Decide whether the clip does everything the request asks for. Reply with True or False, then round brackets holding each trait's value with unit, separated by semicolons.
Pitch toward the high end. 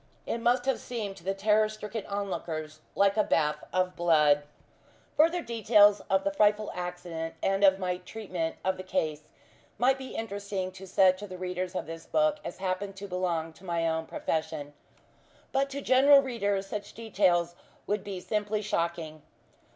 True (195 Hz)